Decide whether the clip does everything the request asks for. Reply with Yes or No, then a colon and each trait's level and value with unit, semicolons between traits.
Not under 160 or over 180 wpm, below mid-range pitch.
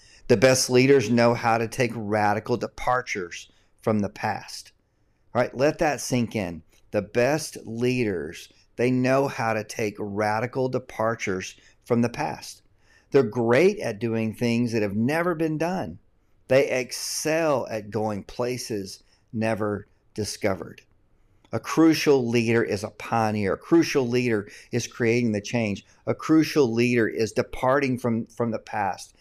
No: average, 145 wpm; low, 115 Hz